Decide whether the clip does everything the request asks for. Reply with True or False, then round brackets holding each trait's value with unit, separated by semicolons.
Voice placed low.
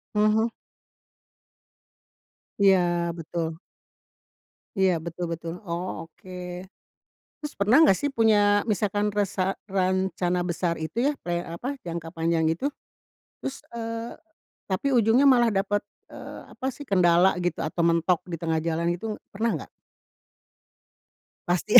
False (185 Hz)